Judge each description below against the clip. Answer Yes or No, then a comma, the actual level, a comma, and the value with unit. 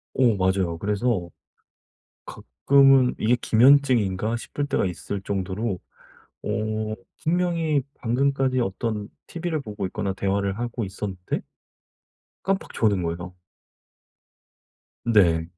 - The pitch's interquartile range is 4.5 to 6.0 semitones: Yes, average, 5.3 semitones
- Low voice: Yes, low, 110 Hz